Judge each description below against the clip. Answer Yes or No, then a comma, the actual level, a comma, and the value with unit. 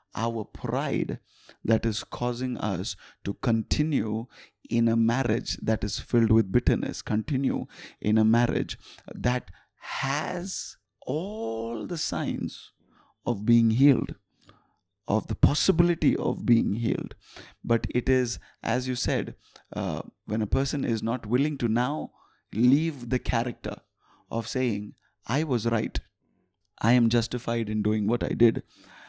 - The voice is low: Yes, low, 115 Hz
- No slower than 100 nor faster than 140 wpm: Yes, slow, 135 wpm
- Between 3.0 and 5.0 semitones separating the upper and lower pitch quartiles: No, narrow, 2.5 semitones